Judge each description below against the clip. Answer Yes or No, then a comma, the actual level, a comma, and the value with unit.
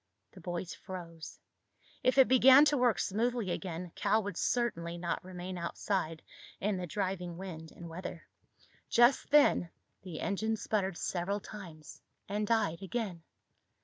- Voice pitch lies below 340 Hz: Yes, high, 190 Hz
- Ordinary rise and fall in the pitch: Yes, average, 4.3 semitones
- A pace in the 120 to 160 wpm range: Yes, average, 140 wpm